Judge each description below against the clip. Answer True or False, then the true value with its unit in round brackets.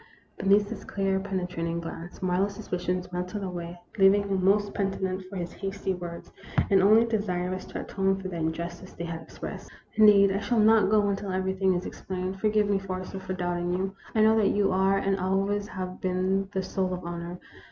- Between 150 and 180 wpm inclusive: False (195 wpm)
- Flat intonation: True (1.6 semitones)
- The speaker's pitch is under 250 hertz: True (190 Hz)